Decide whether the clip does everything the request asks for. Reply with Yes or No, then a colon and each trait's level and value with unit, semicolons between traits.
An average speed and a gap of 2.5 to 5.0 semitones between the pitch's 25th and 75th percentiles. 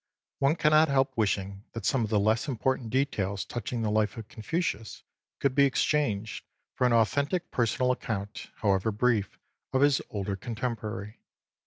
Yes: average, 155 wpm; average, 4.2 semitones